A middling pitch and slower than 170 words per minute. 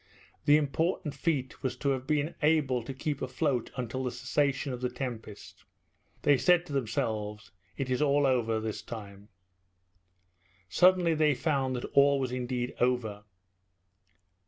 No: low, 130 Hz; average, 145 wpm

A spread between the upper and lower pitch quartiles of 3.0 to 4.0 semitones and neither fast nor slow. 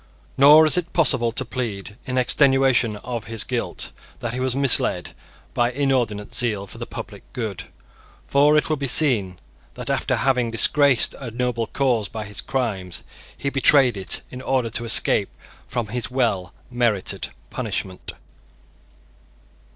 Yes: average, 3.3 semitones; average, 150 wpm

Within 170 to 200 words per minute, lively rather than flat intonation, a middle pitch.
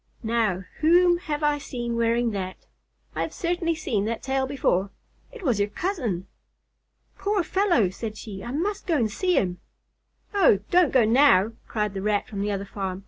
No: average, 180 wpm; wide, 8.3 semitones; high, 235 Hz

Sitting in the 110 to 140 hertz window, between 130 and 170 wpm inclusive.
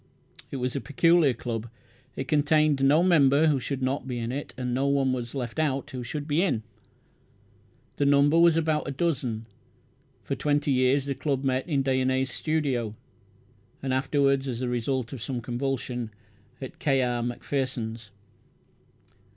Yes: low, 135 Hz; average, 160 wpm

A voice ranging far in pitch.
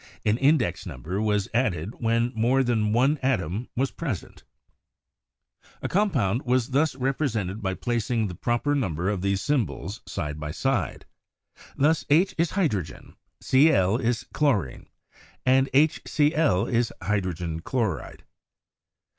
Yes: wide, 5.7 semitones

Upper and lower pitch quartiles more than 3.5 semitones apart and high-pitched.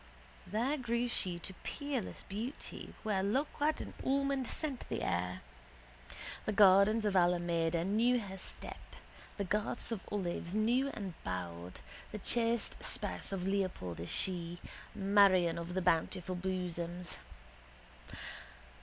Yes: average, 4.8 semitones; high, 195 Hz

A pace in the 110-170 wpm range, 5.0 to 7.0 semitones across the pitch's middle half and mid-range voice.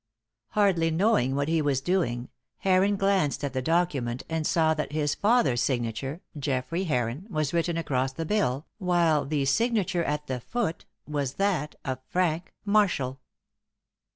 Yes: average, 150 wpm; wide, 5.4 semitones; medium, 155 Hz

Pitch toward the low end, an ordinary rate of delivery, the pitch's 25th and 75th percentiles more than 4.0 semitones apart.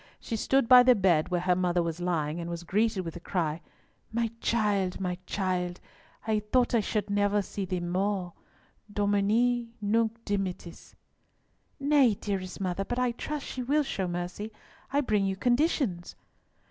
No: high, 200 Hz; average, 160 wpm; average, 4.5 semitones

